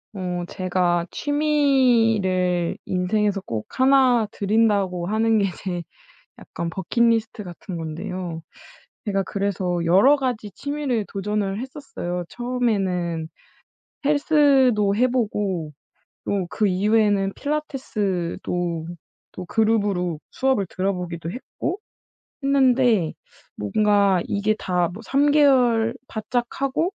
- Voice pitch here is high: Yes, high, 205 Hz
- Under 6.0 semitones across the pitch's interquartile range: Yes, wide, 5.5 semitones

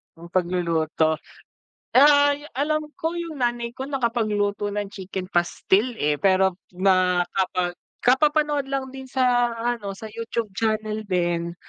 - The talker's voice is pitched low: No, high, 215 Hz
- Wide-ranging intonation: Yes, wide, 6.2 semitones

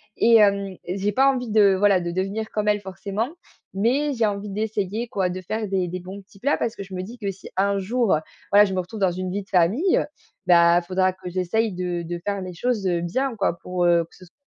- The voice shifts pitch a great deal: No, average, 2.9 semitones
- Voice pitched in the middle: No, high, 195 Hz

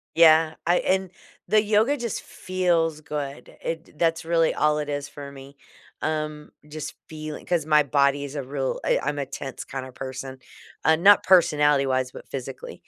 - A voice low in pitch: No, medium, 150 Hz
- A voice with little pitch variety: No, average, 3.1 semitones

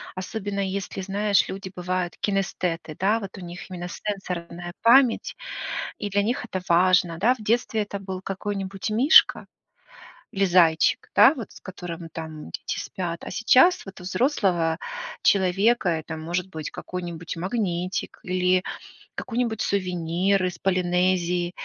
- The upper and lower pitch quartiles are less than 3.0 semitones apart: Yes, narrow, 2.6 semitones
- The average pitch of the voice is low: No, medium, 185 Hz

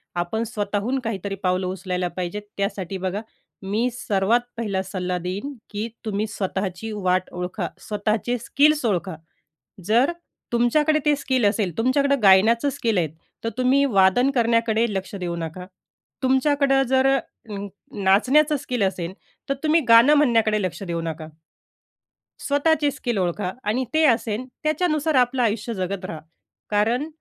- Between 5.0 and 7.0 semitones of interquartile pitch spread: Yes, wide, 5.4 semitones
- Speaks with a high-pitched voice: Yes, high, 220 Hz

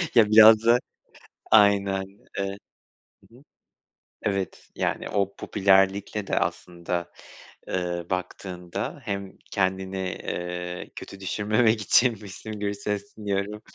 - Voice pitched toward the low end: Yes, low, 100 Hz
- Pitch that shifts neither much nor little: No, narrow, 2.1 semitones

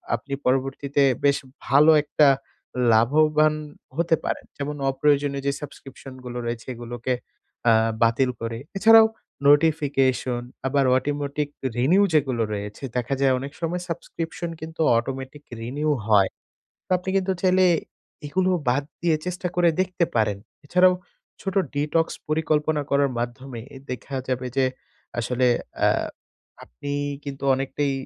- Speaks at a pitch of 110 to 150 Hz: Yes, medium, 140 Hz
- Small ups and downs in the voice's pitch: No, average, 3.7 semitones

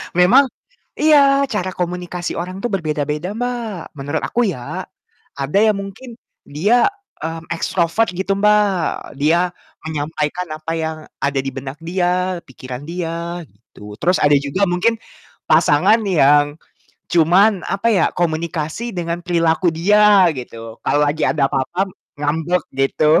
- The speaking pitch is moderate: Yes, medium, 170 Hz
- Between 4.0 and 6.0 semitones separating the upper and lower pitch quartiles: Yes, average, 4.4 semitones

